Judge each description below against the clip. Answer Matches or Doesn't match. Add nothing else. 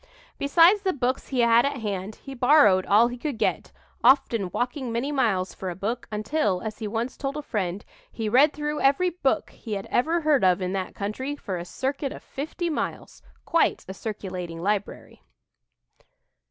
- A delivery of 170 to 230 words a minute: Matches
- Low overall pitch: Doesn't match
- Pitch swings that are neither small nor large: Doesn't match